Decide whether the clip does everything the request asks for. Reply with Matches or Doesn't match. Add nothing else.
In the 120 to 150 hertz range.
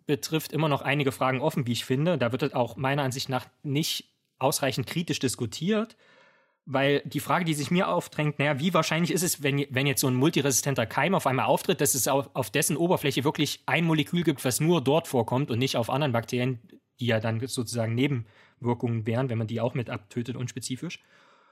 Matches